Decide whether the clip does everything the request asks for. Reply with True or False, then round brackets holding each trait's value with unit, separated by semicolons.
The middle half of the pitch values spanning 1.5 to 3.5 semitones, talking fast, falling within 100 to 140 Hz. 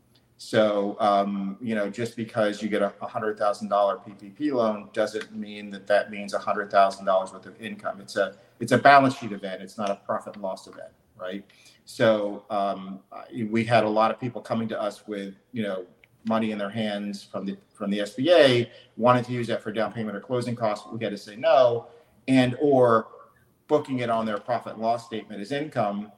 False (2.7 semitones; 195 wpm; 110 Hz)